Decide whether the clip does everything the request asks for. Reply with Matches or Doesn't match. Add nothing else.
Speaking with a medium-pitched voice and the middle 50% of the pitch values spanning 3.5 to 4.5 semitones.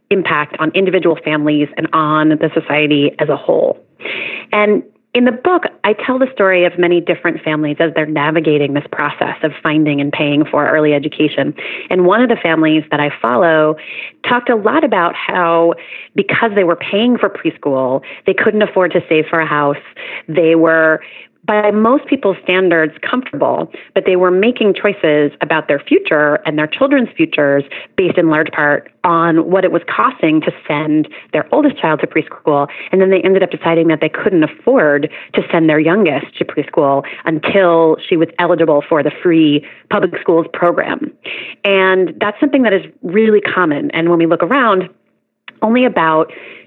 Matches